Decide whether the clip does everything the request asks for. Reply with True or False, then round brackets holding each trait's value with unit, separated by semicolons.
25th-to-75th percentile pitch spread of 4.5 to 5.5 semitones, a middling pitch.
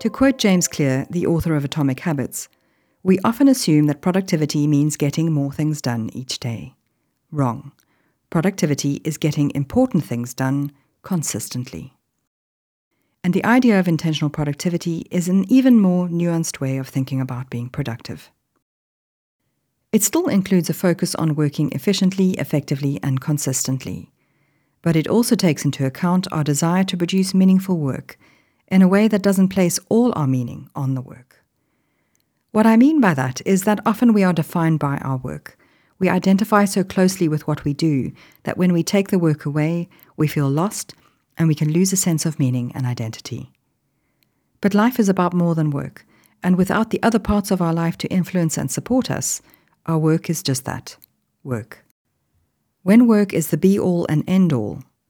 True (5.0 semitones; 165 Hz)